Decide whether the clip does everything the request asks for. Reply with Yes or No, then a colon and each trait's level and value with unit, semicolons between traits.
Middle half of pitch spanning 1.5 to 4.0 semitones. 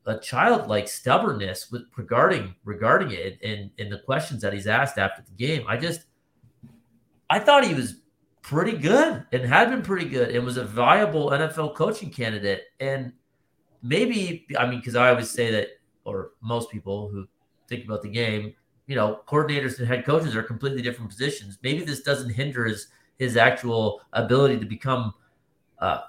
No: average, 4.4 semitones